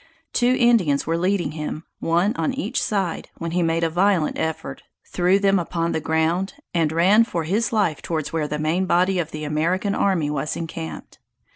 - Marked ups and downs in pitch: No, average, 3.4 semitones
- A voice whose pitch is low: No, medium, 170 Hz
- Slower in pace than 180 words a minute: No, average, 185 wpm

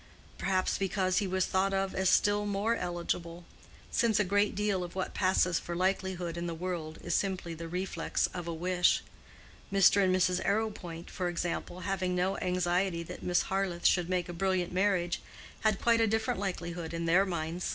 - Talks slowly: No, average, 185 wpm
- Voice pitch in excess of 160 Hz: Yes, medium, 185 Hz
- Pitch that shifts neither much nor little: No, narrow, 2.0 semitones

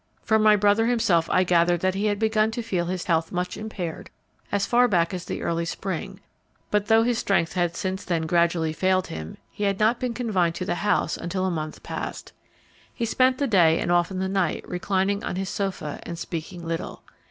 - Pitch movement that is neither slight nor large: Yes, average, 3.5 semitones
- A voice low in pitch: No, medium, 185 Hz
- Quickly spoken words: Yes, fast, 210 wpm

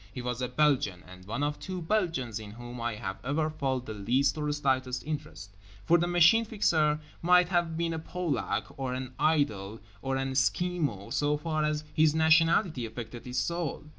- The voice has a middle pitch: Yes, medium, 145 Hz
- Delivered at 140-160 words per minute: No, average, 185 wpm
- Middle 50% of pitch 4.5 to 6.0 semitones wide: Yes, average, 4.8 semitones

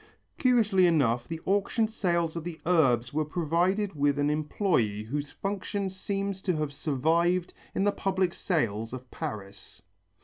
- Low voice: No, medium, 165 Hz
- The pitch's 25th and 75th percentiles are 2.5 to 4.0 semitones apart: No, average, 5.1 semitones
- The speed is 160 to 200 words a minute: No, average, 145 wpm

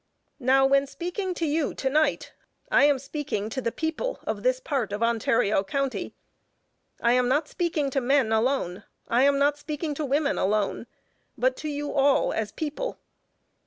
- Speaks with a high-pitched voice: Yes, very high, 275 Hz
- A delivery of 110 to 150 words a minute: No, average, 170 wpm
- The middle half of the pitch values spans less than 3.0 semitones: No, average, 3.7 semitones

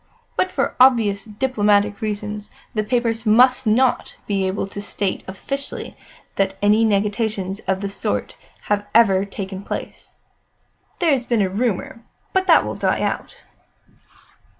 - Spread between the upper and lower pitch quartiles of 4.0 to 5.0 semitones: No, average, 3.0 semitones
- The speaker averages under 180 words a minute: Yes, average, 140 wpm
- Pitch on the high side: Yes, high, 210 Hz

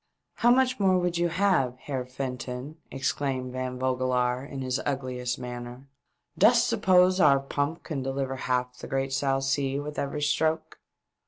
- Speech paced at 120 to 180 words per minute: Yes, average, 170 wpm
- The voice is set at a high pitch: No, low, 135 Hz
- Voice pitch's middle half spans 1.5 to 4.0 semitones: Yes, average, 2.7 semitones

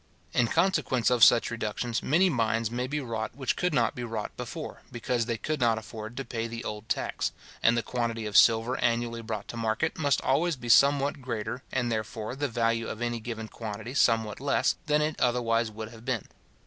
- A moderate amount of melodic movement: No, narrow, 2.3 semitones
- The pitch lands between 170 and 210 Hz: No, low, 115 Hz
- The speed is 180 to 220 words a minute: Yes, average, 200 wpm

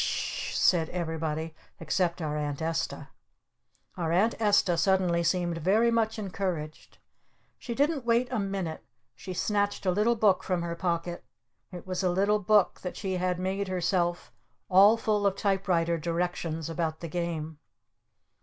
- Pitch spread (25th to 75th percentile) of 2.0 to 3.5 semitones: Yes, average, 3.2 semitones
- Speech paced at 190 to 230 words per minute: No, average, 155 wpm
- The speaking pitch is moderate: Yes, medium, 180 Hz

